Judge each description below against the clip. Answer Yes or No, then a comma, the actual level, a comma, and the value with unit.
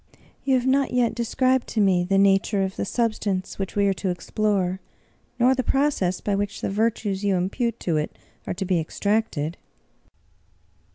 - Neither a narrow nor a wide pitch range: Yes, average, 3.8 semitones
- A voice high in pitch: Yes, high, 200 Hz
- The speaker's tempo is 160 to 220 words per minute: Yes, average, 180 wpm